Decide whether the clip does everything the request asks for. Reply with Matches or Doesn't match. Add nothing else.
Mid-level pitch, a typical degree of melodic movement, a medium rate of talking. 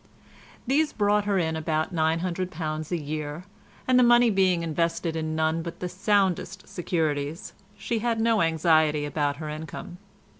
Matches